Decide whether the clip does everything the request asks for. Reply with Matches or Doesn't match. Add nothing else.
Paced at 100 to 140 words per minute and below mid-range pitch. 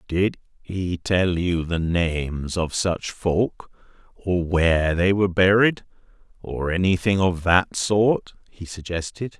Matches